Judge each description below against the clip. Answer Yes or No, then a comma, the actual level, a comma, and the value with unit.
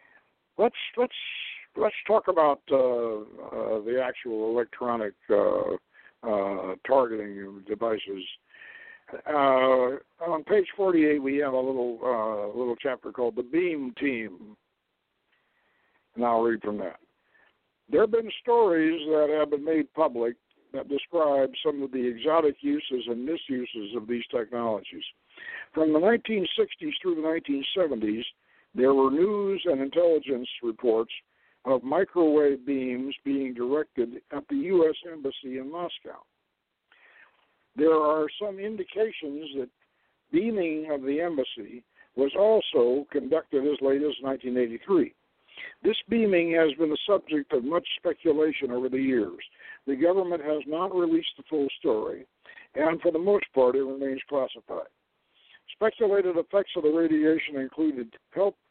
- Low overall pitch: No, medium, 150 Hz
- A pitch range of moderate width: No, wide, 6.2 semitones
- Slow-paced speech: Yes, slow, 130 wpm